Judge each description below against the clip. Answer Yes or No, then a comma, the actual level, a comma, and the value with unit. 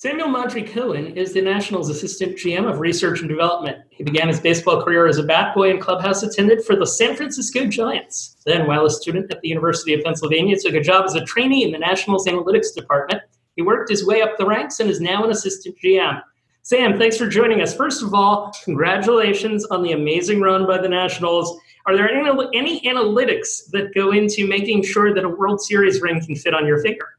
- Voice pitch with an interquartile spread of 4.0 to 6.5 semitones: Yes, average, 4.3 semitones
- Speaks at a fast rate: Yes, fast, 215 wpm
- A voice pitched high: Yes, high, 195 Hz